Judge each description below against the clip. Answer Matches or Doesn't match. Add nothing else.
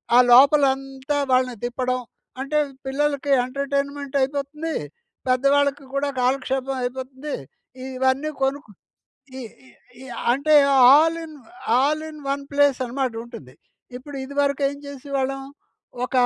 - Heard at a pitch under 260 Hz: Doesn't match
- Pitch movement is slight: Matches